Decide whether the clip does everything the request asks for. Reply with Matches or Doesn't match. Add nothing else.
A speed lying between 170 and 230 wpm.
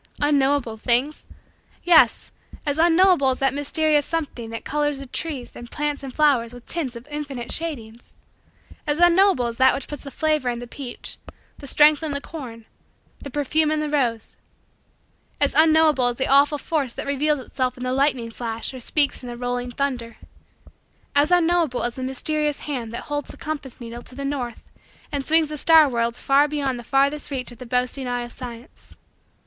Matches